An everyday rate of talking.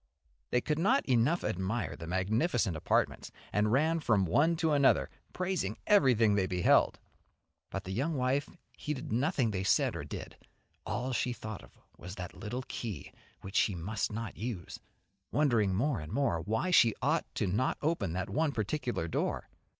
Yes: average, 165 wpm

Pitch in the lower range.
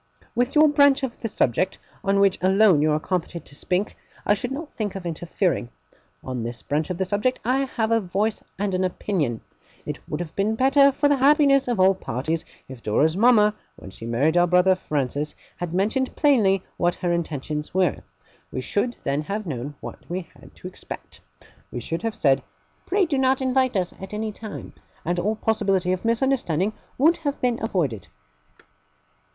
No: high, 195 Hz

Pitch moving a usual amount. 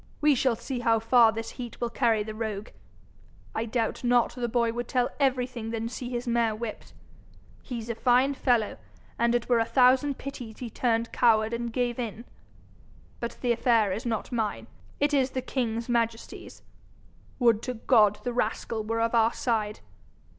No: narrow, 1.6 semitones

